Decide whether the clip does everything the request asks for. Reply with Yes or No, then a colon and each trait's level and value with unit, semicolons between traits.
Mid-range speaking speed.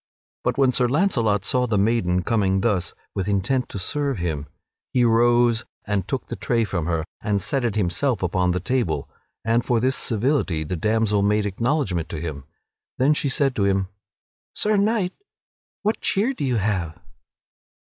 Yes: average, 170 wpm